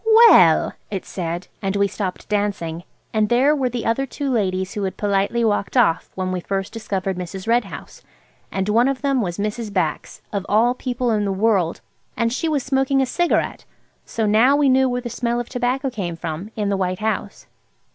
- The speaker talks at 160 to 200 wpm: Yes, average, 195 wpm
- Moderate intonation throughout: Yes, average, 4.5 semitones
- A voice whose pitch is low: No, high, 215 Hz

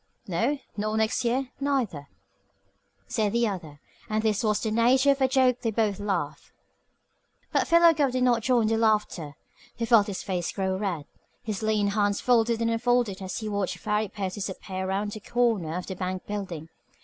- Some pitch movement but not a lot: Yes, average, 3.7 semitones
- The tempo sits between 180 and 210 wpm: Yes, average, 190 wpm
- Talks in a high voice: Yes, high, 215 Hz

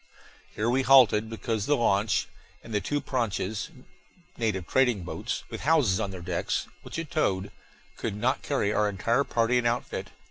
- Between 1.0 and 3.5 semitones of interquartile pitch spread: No, average, 4.3 semitones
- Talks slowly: No, average, 170 wpm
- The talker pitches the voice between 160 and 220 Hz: No, low, 115 Hz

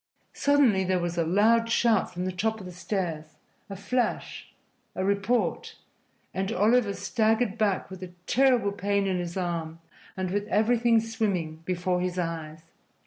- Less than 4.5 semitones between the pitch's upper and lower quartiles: Yes, average, 3.8 semitones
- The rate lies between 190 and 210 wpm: No, average, 155 wpm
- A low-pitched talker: No, high, 195 Hz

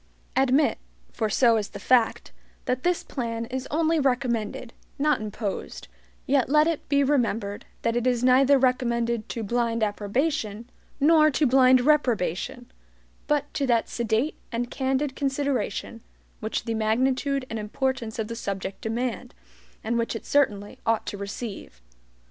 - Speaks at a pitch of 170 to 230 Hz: No, high, 245 Hz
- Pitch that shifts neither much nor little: Yes, average, 3.5 semitones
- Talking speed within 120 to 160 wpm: Yes, average, 145 wpm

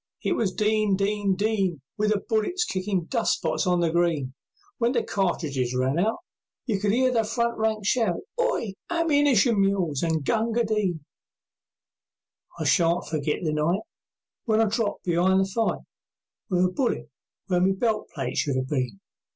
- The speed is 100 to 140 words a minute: No, average, 165 wpm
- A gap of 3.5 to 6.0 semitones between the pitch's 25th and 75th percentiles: Yes, average, 4.6 semitones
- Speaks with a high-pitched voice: Yes, high, 195 Hz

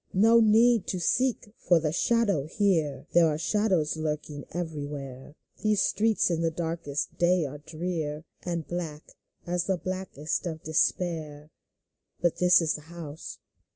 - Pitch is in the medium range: Yes, medium, 165 Hz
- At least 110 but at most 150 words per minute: Yes, average, 145 wpm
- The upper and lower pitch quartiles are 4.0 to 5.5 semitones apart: No, average, 3.5 semitones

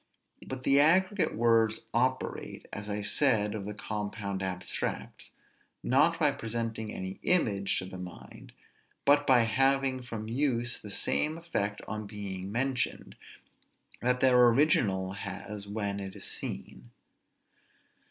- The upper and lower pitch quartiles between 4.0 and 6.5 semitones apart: Yes, average, 4.6 semitones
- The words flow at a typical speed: No, slow, 130 wpm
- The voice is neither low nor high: No, low, 110 Hz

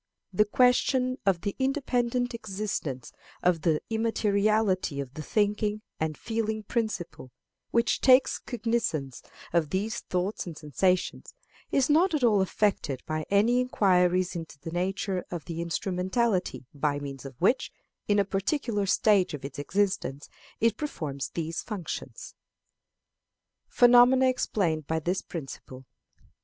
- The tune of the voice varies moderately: No, wide, 5.8 semitones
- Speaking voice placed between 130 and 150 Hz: No, high, 195 Hz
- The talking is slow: Yes, slow, 130 wpm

